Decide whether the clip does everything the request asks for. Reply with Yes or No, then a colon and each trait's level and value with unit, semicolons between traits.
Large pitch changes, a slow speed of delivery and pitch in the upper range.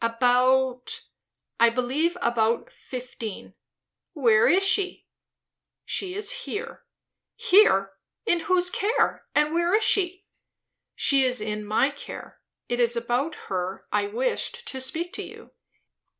Yes: wide, 7.8 semitones; slow, 125 wpm; very high, 270 Hz